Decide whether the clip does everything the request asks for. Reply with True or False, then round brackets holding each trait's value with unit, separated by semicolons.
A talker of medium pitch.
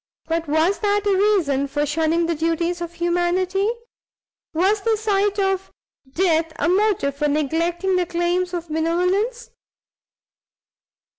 False (345 Hz)